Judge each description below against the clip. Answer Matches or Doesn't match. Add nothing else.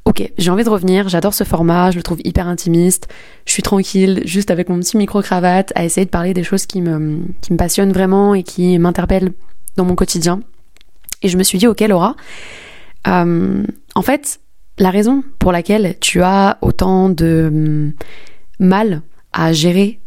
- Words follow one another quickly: Doesn't match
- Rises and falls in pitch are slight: Matches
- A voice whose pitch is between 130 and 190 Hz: Matches